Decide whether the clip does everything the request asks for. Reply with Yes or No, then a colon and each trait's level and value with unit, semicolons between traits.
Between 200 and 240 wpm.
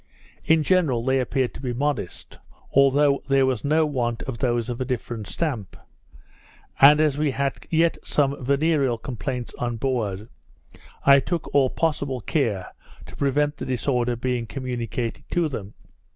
No: average, 150 wpm